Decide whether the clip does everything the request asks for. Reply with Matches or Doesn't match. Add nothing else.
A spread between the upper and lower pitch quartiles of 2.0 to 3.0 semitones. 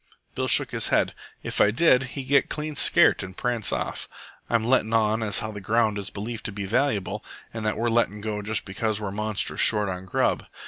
Matches